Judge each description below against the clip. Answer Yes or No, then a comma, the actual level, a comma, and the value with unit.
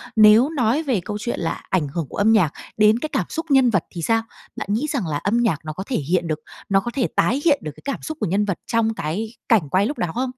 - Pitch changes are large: Yes, wide, 5.7 semitones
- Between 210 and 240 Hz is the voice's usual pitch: Yes, high, 215 Hz